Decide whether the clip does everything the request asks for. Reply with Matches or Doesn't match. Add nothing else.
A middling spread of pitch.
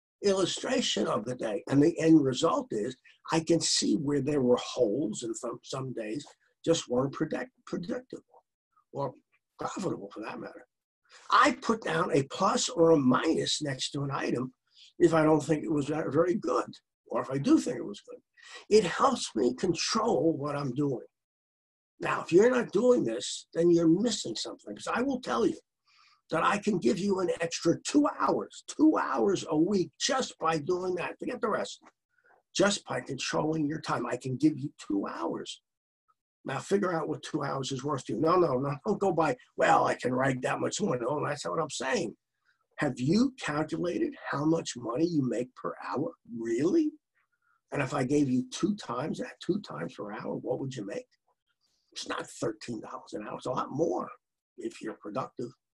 Doesn't match